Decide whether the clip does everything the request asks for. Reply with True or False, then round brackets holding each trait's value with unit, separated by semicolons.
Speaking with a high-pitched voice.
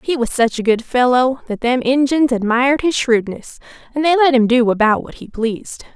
True (250 Hz)